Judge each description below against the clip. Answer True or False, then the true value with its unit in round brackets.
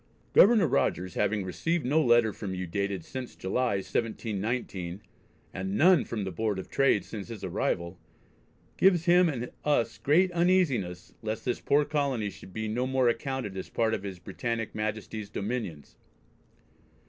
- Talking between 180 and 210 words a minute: False (155 wpm)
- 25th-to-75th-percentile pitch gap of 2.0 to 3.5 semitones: False (5.4 semitones)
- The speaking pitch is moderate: False (110 Hz)